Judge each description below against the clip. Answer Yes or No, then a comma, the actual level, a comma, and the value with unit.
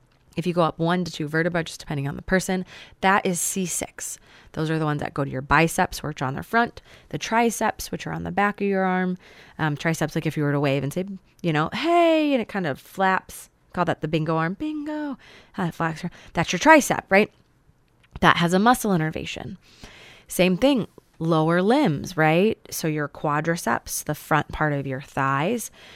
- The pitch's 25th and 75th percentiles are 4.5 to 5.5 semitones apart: No, average, 3.9 semitones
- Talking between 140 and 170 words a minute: No, average, 200 wpm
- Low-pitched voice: No, medium, 170 Hz